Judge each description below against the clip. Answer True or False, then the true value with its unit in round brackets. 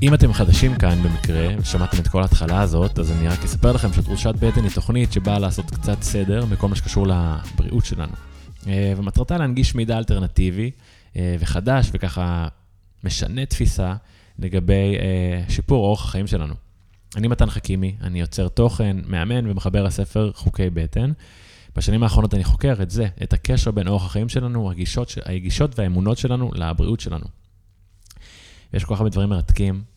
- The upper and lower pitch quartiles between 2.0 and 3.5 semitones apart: True (3.2 semitones)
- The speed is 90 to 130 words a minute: False (150 wpm)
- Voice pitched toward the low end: True (100 Hz)